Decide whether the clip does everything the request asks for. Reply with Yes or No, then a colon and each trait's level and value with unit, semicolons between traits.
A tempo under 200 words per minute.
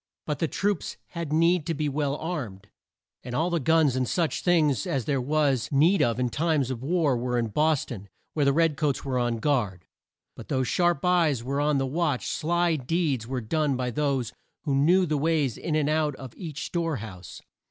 No: fast, 205 wpm